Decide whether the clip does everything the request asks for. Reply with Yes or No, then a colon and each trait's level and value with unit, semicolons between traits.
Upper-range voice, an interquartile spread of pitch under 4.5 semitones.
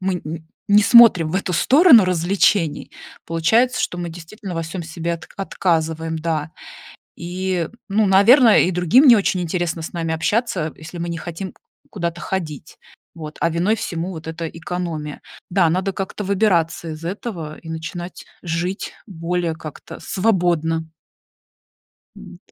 No: medium, 175 Hz; average, 3.0 semitones